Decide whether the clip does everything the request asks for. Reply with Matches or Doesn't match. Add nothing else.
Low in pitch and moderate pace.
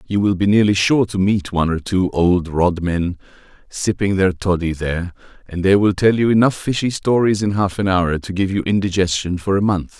Doesn't match